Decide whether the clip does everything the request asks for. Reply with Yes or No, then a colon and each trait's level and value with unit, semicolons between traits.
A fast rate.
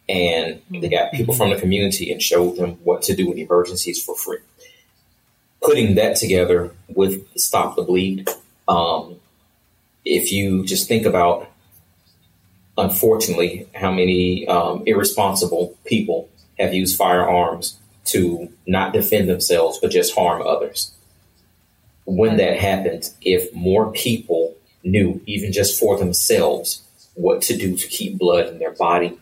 No: average, 140 wpm